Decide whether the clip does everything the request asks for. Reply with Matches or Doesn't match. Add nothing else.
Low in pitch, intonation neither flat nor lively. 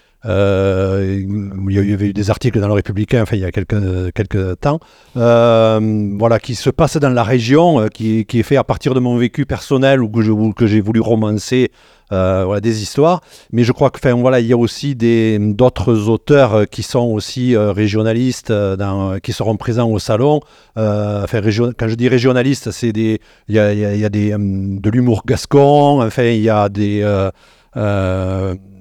Matches